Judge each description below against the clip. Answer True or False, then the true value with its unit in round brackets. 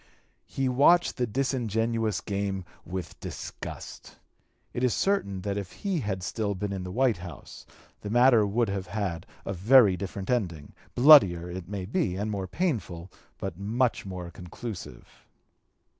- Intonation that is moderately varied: True (4.7 semitones)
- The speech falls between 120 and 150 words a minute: False (160 wpm)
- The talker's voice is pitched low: True (100 Hz)